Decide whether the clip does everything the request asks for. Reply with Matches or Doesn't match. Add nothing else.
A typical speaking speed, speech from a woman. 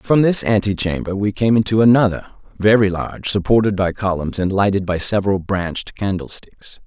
Doesn't match